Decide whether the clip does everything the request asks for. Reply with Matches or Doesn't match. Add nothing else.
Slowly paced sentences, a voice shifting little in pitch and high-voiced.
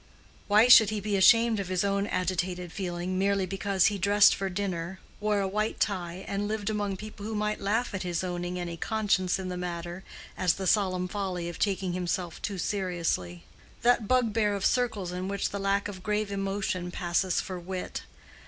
Doesn't match